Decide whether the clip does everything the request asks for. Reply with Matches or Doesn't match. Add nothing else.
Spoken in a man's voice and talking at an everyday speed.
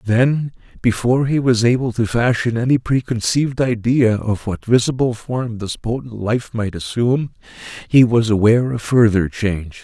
Matches